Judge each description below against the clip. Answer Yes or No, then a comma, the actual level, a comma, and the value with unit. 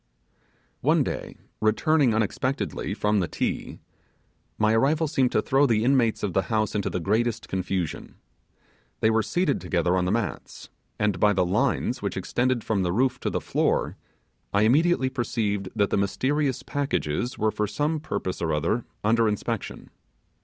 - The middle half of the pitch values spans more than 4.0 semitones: Yes, average, 4.6 semitones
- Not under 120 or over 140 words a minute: No, average, 160 wpm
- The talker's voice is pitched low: Yes, low, 110 Hz